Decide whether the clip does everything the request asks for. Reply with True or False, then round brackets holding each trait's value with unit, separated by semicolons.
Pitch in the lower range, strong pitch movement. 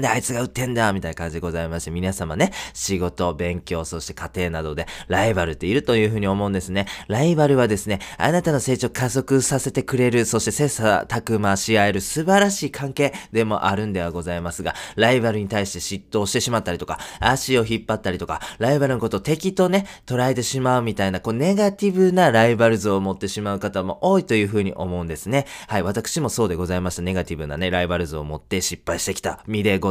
True (105 Hz; 5.8 semitones)